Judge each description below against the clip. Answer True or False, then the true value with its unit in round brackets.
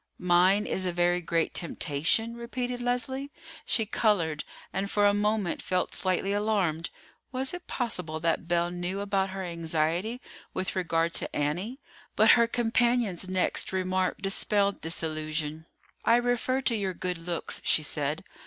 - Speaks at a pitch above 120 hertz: True (185 Hz)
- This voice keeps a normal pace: True (150 wpm)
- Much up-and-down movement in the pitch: False (4.8 semitones)